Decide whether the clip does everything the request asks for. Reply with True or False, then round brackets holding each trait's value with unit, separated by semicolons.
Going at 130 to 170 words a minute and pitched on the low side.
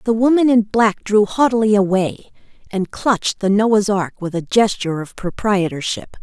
False (165 wpm; 205 Hz)